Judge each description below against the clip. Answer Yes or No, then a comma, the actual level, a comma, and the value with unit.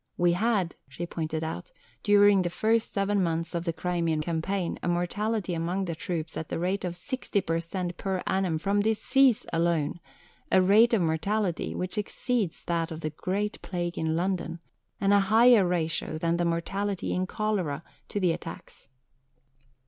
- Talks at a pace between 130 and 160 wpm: No, average, 170 wpm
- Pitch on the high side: No, medium, 180 Hz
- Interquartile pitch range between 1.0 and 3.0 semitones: No, average, 3.4 semitones